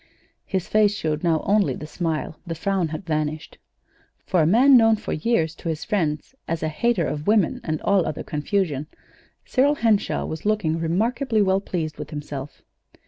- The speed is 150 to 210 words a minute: Yes, average, 175 wpm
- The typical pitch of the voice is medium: Yes, medium, 170 Hz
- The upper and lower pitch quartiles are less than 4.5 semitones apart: No, average, 5.2 semitones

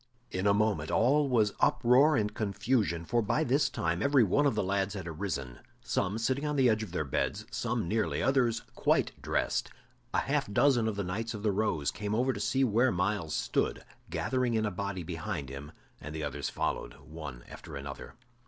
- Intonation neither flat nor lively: No, wide, 6.1 semitones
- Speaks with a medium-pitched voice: No, low, 105 Hz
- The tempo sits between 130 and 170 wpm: No, average, 195 wpm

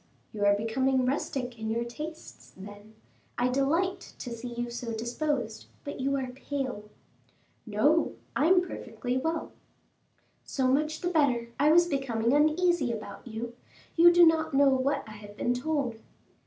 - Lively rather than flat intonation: No, average, 4.5 semitones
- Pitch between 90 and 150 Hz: No, very high, 260 Hz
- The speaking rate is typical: Yes, average, 155 wpm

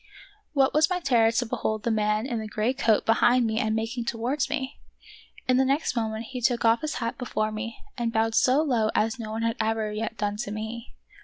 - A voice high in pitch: Yes, high, 230 Hz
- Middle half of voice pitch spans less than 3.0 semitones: Yes, narrow, 2.4 semitones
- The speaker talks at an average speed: No, fast, 225 wpm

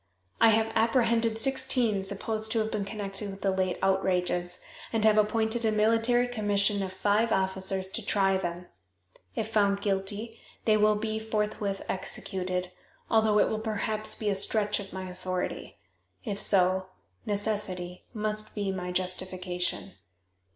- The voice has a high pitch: Yes, high, 205 Hz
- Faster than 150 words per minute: No, average, 145 wpm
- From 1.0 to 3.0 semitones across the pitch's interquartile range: Yes, narrow, 2.5 semitones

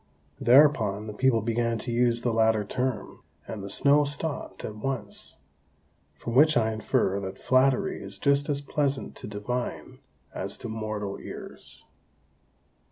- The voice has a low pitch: Yes, low, 115 Hz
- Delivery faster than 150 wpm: No, average, 145 wpm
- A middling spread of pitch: Yes, average, 4.2 semitones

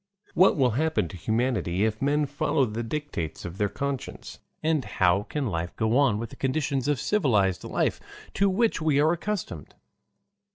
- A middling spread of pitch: No, wide, 6.3 semitones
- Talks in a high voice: No, low, 130 Hz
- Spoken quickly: No, average, 170 wpm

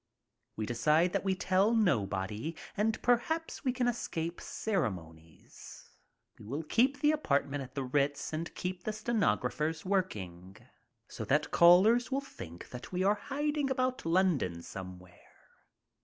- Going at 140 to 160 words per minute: Yes, average, 145 wpm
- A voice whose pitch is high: No, medium, 175 Hz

